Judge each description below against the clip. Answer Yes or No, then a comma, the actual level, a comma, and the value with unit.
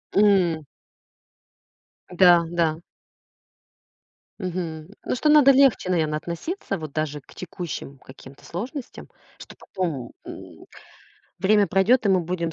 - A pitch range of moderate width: Yes, average, 4.3 semitones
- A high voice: No, medium, 180 Hz